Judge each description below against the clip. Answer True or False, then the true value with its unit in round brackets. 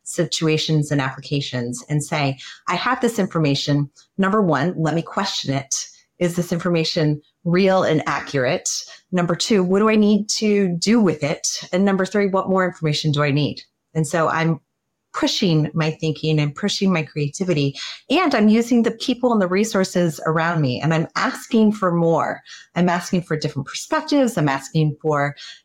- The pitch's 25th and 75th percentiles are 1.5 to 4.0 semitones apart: False (4.5 semitones)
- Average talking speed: True (170 wpm)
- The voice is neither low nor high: True (170 Hz)